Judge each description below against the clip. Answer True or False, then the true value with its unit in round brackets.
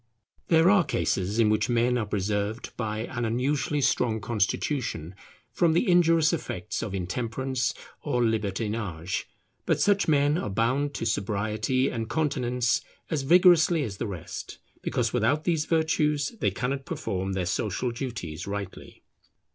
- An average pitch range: False (5.7 semitones)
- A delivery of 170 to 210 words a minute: False (140 wpm)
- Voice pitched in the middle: False (120 Hz)